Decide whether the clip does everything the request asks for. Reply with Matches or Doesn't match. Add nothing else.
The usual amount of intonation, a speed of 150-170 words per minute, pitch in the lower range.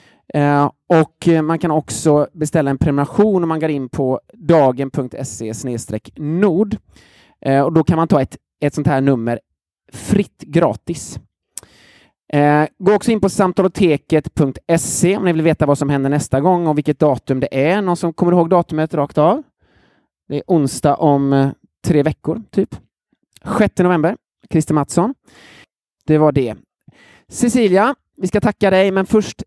Doesn't match